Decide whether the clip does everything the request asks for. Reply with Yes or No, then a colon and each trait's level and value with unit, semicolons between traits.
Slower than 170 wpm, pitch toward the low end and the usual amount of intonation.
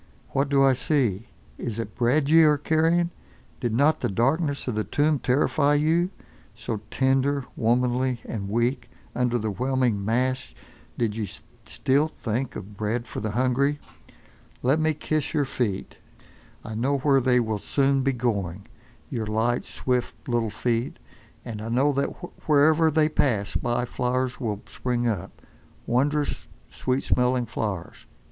Yes: average, 145 wpm; low, 125 Hz; average, 3.7 semitones